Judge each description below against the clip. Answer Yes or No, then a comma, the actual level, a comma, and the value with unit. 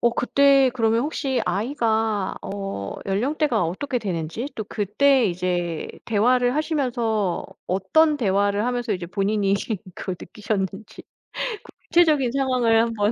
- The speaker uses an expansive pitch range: No, average, 4.6 semitones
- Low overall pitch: No, high, 225 Hz